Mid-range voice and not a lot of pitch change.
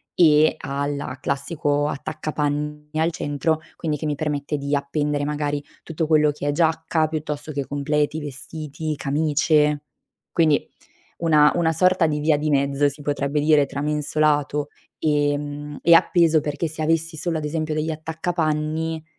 Yes: medium, 150 Hz; narrow, 1.5 semitones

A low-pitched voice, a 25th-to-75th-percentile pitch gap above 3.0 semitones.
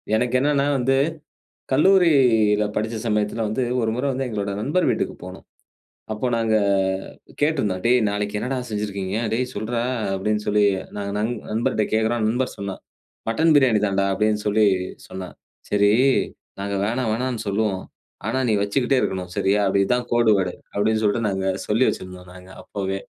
Yes: low, 110 Hz; average, 3.4 semitones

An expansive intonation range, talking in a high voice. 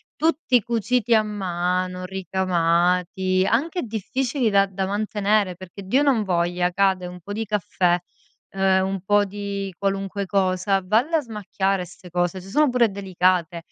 No: average, 2.7 semitones; high, 195 Hz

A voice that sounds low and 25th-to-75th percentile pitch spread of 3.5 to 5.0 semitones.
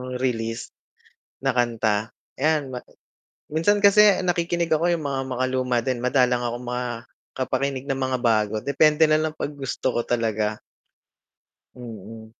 Yes: low, 130 Hz; average, 4.1 semitones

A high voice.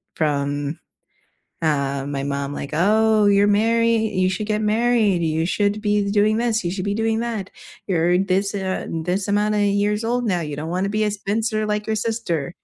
Yes: high, 205 Hz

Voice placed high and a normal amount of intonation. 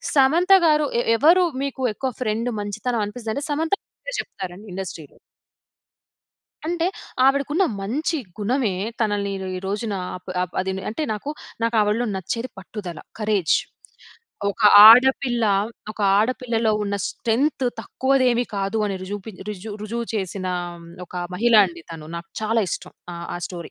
Yes: high, 220 Hz; average, 4.9 semitones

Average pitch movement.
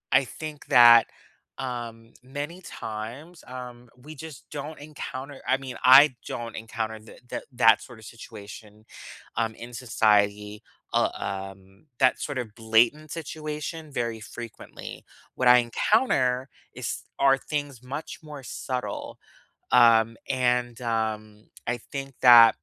Yes: average, 3.5 semitones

